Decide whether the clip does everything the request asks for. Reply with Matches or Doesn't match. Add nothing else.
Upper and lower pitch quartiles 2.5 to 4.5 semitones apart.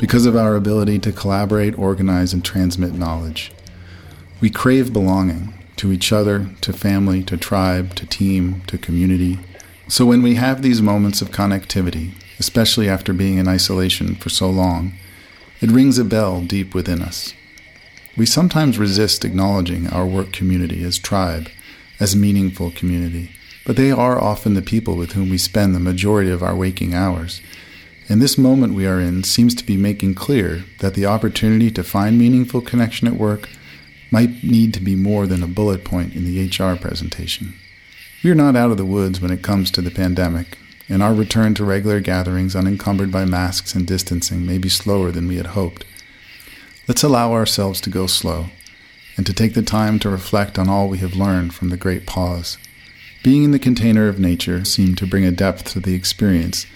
Matches